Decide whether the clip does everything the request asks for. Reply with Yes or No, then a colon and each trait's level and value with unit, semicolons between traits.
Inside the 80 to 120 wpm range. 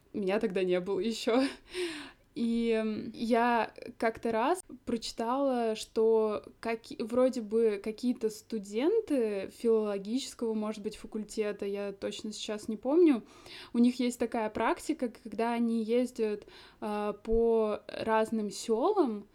Yes: slow, 110 wpm